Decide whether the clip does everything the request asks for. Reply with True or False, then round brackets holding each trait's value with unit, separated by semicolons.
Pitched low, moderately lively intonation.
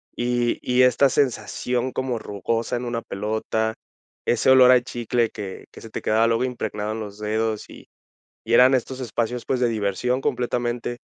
False (120 Hz; 2.2 semitones)